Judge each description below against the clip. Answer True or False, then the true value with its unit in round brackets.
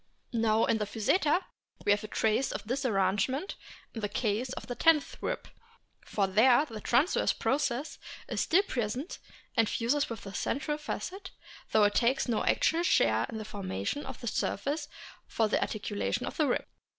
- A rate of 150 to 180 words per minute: True (175 wpm)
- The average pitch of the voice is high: True (230 Hz)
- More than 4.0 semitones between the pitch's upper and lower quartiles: True (5.3 semitones)